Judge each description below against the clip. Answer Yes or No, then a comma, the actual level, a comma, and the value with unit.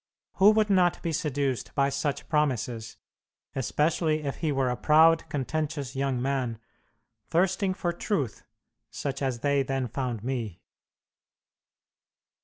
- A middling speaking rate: No, slow, 125 wpm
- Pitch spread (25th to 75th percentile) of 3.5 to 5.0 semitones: Yes, average, 3.9 semitones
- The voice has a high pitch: No, medium, 140 Hz